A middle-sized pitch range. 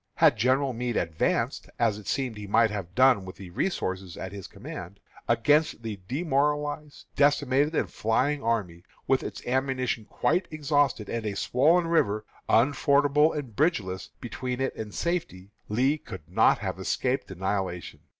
No: wide, 6.2 semitones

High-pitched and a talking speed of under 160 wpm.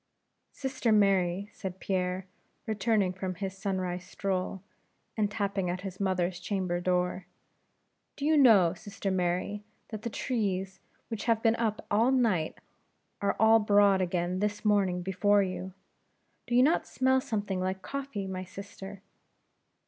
Yes: high, 195 Hz; average, 140 wpm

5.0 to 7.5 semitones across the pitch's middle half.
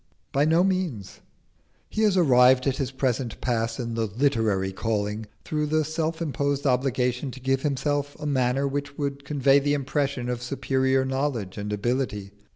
No: average, 2.9 semitones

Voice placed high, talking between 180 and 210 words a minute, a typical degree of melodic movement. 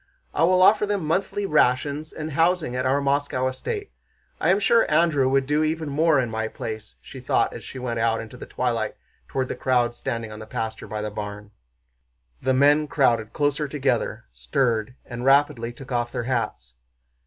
No: low, 130 Hz; average, 190 wpm; average, 4.7 semitones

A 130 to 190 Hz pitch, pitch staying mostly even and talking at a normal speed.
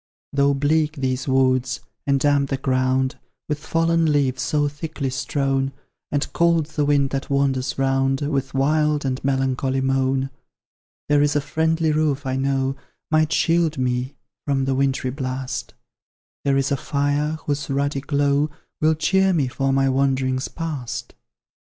Yes: medium, 140 Hz; narrow, 1.9 semitones; average, 150 wpm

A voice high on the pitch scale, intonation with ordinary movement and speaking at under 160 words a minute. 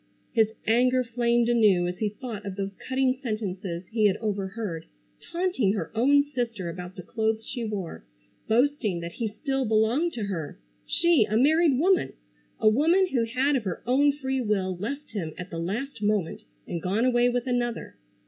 No: high, 225 Hz; average, 4.6 semitones; average, 175 wpm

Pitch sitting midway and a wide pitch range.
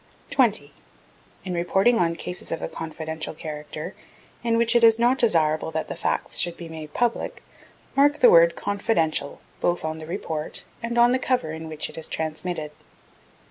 Yes: medium, 170 Hz; wide, 6.7 semitones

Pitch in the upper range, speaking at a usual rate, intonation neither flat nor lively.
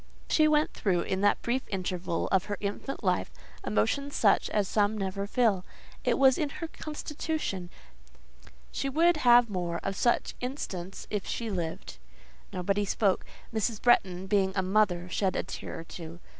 Yes: high, 205 Hz; average, 160 wpm; average, 4.8 semitones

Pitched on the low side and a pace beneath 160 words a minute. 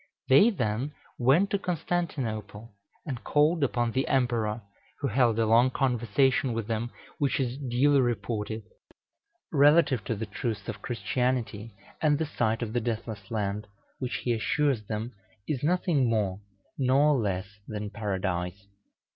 Yes: low, 120 Hz; average, 140 wpm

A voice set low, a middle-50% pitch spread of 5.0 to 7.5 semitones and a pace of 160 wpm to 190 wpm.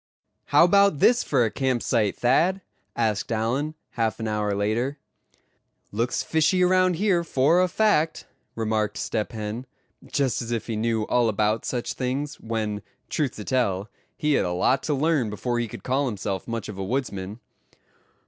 Yes: low, 120 Hz; average, 5.3 semitones; average, 170 wpm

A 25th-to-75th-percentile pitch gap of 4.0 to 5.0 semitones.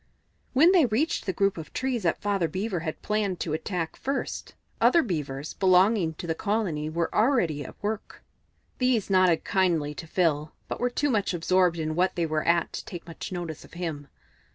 Yes: average, 4.7 semitones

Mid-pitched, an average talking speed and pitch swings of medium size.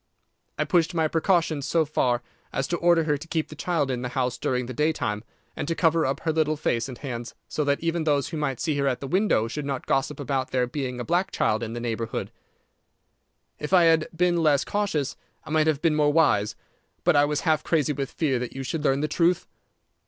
No: medium, 150 Hz; fast, 230 wpm; average, 3.8 semitones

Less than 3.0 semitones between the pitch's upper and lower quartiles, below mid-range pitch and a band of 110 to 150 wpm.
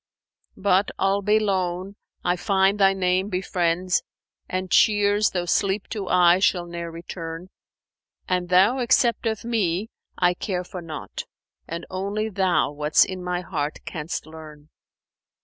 No: narrow, 2.5 semitones; medium, 185 Hz; average, 145 wpm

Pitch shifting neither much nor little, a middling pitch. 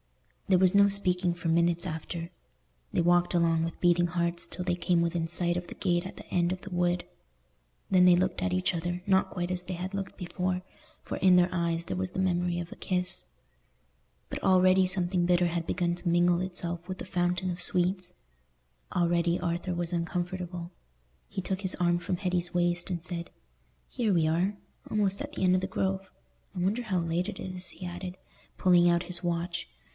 No: narrow, 1.1 semitones; medium, 175 Hz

